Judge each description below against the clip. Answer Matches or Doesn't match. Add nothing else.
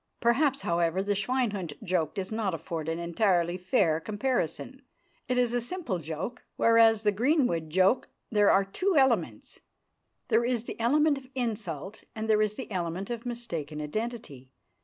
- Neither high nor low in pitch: Doesn't match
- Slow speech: Doesn't match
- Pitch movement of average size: Doesn't match